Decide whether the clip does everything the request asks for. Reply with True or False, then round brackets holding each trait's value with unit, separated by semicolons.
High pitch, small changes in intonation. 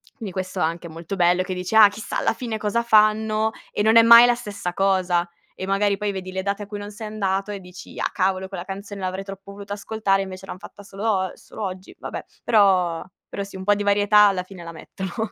True (195 Hz; 2.0 semitones)